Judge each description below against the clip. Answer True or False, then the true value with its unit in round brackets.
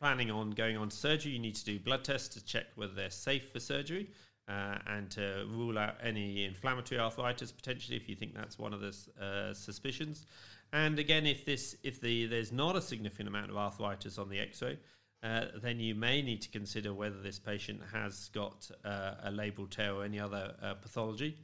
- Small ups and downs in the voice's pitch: False (3.8 semitones)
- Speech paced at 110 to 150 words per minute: False (205 wpm)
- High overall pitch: False (110 Hz)